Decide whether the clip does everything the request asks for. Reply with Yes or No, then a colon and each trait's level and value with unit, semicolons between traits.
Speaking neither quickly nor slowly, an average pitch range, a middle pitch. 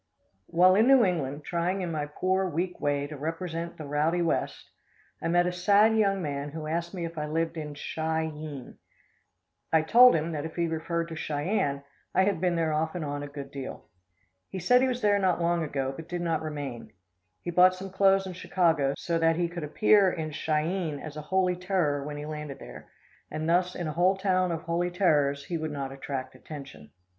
No: fast, 215 wpm; average, 3.3 semitones; medium, 165 Hz